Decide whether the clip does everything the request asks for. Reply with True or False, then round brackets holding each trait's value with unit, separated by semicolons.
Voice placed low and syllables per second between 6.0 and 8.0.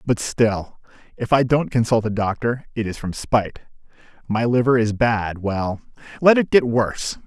False (115 Hz; 4.7 syllables/s)